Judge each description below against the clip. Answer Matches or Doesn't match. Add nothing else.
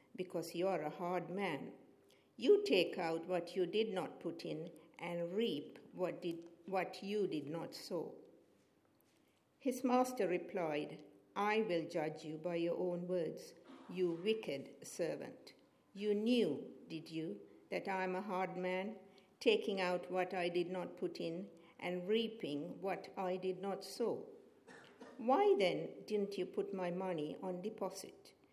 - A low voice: Doesn't match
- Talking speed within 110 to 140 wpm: Doesn't match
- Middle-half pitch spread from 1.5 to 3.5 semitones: Matches